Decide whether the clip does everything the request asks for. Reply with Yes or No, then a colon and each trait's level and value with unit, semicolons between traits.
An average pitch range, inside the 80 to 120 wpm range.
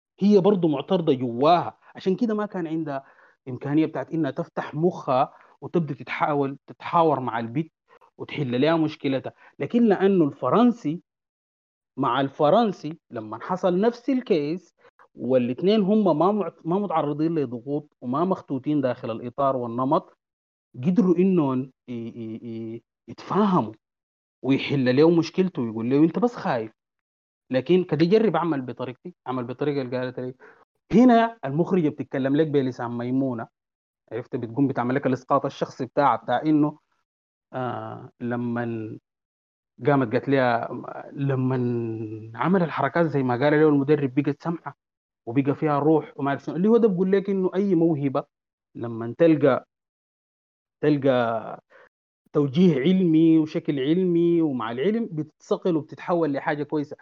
No: average, 5.0 semitones; average, 130 wpm